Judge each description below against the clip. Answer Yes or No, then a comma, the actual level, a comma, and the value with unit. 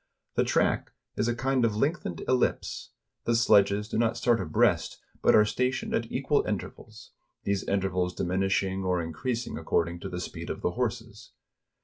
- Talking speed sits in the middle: Yes, average, 160 wpm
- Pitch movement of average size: Yes, average, 4.5 semitones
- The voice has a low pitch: Yes, low, 105 Hz